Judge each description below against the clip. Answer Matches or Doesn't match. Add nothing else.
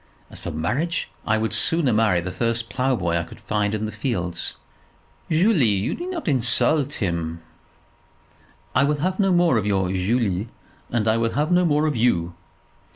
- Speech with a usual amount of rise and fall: Doesn't match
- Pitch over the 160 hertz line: Doesn't match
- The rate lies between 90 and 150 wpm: Doesn't match